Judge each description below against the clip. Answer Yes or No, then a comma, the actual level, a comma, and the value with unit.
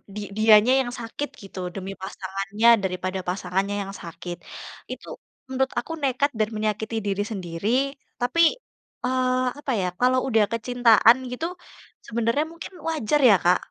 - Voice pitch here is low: No, high, 220 Hz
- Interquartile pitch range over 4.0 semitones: Yes, average, 4.5 semitones